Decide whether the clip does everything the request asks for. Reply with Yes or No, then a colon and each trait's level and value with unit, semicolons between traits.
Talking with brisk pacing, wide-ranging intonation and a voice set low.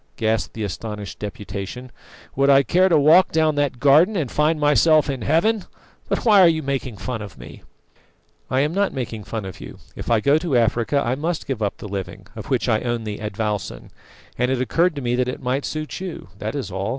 Yes: fast, 220 wpm; wide, 5.9 semitones; low, 130 Hz